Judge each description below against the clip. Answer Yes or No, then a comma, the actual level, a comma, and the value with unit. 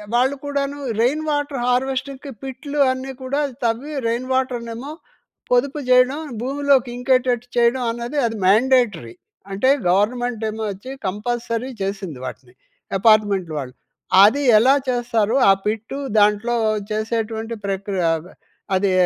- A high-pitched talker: Yes, high, 240 Hz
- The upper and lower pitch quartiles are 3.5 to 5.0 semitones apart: Yes, average, 3.8 semitones